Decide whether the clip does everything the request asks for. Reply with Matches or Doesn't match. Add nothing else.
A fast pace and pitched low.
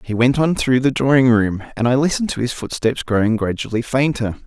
Matches